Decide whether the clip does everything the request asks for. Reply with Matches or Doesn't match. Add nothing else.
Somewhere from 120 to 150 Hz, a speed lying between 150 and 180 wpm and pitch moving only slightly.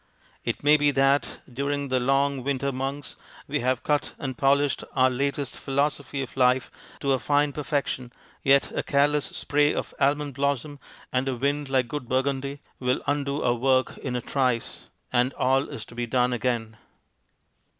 Matches